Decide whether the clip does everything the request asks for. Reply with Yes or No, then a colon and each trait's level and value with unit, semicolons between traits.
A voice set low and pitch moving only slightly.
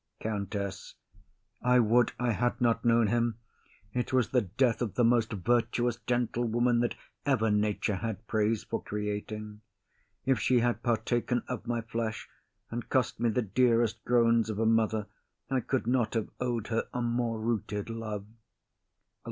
Yes: low, 115 Hz; narrow, 2.0 semitones